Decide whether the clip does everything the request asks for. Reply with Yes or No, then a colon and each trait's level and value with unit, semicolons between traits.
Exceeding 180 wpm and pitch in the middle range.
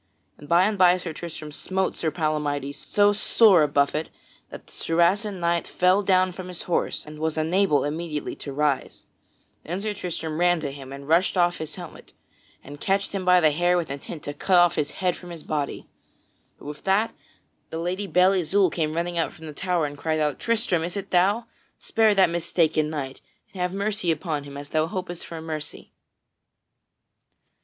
Yes: average, 195 wpm; medium, 170 Hz